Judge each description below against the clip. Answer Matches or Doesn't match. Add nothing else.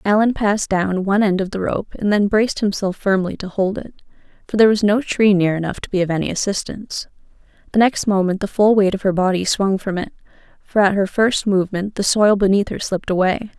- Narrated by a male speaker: Doesn't match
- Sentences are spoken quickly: Matches